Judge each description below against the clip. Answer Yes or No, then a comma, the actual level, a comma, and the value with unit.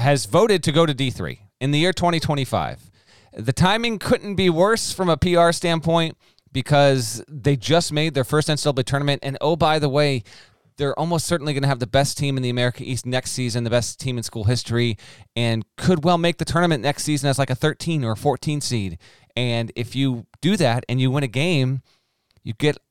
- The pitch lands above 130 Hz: Yes, medium, 140 Hz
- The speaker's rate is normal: No, fast, 210 wpm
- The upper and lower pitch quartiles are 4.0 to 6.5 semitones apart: Yes, average, 4.6 semitones